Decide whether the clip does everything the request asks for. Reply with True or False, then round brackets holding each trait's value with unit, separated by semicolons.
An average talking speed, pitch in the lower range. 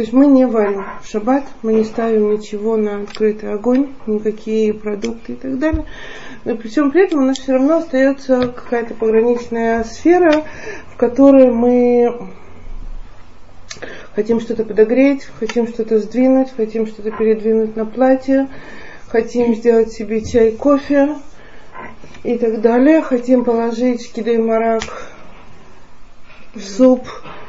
False (130 wpm; 235 Hz)